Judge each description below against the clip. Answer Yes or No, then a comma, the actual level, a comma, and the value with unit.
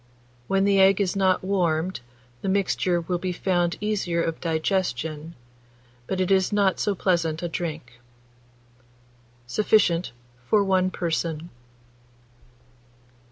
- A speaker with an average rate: No, slow, 115 wpm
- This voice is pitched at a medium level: Yes, medium, 180 Hz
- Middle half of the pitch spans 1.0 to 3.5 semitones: Yes, narrow, 2.6 semitones